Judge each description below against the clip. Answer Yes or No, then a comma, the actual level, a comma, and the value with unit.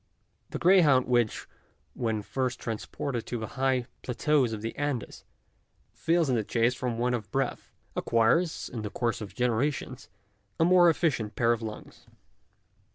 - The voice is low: Yes, low, 125 Hz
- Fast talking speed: No, average, 155 wpm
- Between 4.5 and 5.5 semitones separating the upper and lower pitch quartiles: No, average, 3.6 semitones